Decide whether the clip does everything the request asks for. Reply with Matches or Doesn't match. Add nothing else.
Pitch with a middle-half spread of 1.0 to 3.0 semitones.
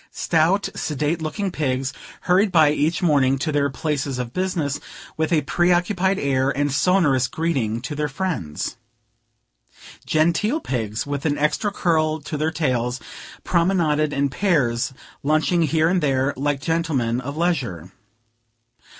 Doesn't match